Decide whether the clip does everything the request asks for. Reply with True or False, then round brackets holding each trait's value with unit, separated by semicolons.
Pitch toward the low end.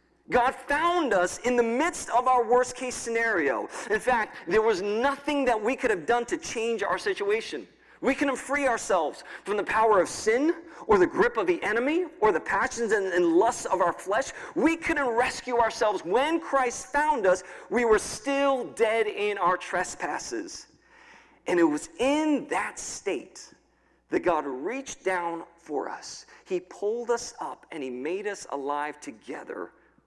False (270 Hz)